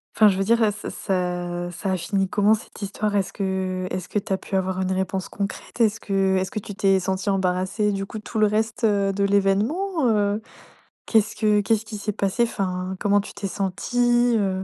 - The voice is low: No, high, 200 Hz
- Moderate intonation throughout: No, narrow, 2.1 semitones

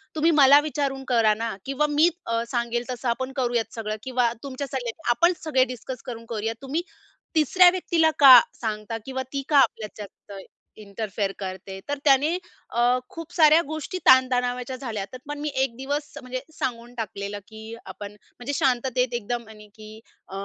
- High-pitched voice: Yes, very high, 250 Hz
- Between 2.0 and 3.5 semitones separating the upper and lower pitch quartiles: No, average, 3.9 semitones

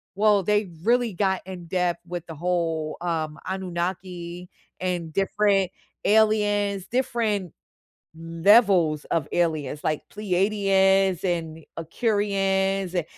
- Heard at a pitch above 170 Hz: Yes, medium, 185 Hz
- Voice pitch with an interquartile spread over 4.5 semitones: No, average, 3.0 semitones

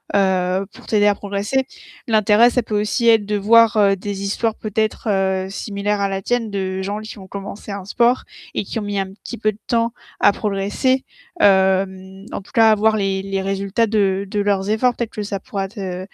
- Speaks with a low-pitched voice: No, high, 205 Hz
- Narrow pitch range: Yes, narrow, 2.0 semitones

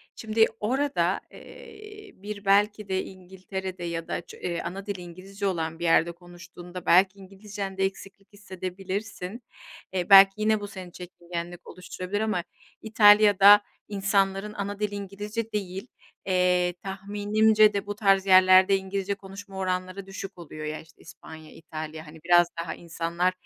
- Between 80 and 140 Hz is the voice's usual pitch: No, high, 195 Hz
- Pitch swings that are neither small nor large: No, narrow, 2.3 semitones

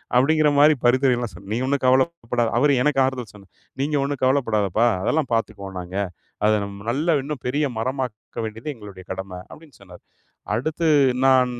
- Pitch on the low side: Yes, low, 125 Hz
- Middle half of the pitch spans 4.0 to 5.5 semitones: Yes, average, 5.1 semitones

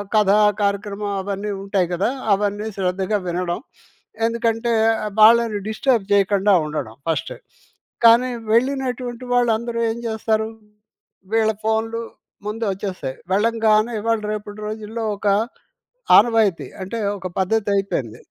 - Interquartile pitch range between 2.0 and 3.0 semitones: Yes, narrow, 2.5 semitones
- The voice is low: No, high, 215 Hz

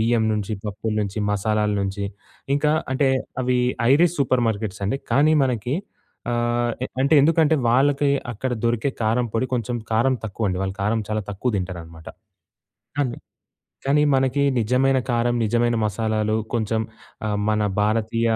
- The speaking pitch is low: Yes, low, 115 Hz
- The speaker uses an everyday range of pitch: Yes, average, 3.5 semitones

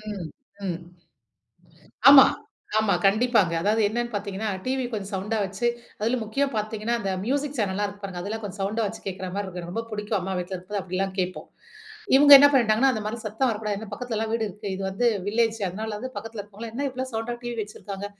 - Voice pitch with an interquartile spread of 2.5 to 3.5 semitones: Yes, average, 2.9 semitones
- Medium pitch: No, high, 215 Hz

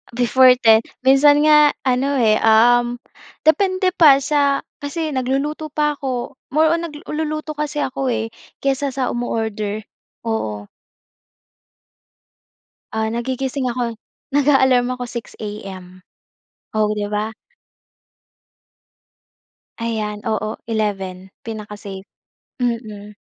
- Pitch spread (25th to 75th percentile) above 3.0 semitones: Yes, average, 4.7 semitones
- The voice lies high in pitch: Yes, high, 245 Hz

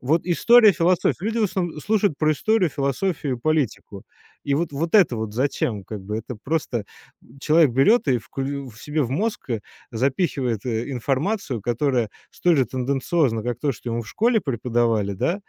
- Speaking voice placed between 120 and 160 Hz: Yes, medium, 140 Hz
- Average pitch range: No, wide, 6.1 semitones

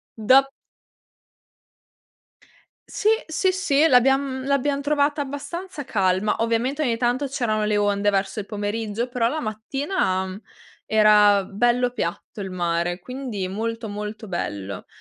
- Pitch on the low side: No, high, 230 Hz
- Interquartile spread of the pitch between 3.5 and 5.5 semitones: Yes, average, 5.1 semitones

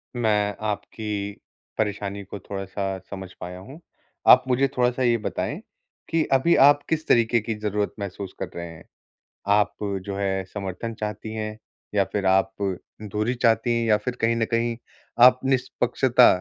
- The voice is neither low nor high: No, low, 105 Hz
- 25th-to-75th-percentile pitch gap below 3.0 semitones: No, average, 3.3 semitones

